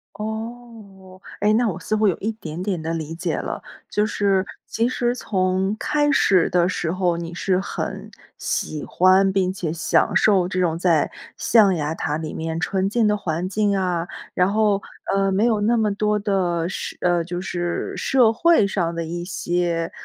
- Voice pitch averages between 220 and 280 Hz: No, high, 190 Hz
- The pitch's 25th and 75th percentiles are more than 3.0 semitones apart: Yes, average, 3.4 semitones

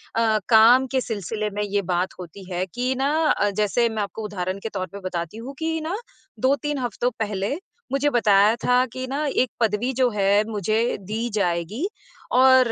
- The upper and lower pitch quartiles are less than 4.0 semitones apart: No, average, 4.3 semitones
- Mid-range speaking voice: No, high, 220 Hz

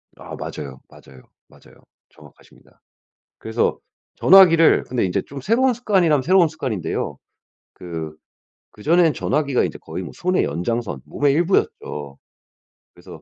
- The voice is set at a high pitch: No, medium, 140 Hz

